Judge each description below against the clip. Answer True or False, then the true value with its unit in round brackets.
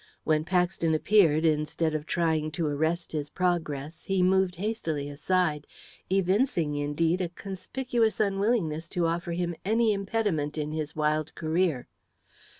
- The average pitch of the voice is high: False (170 Hz)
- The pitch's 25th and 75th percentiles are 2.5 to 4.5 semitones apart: True (3.6 semitones)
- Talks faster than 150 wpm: False (135 wpm)